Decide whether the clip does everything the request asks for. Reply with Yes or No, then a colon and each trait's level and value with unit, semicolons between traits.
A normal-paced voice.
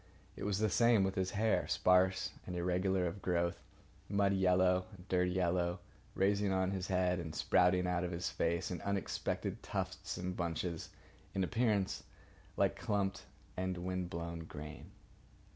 Yes: average, 155 wpm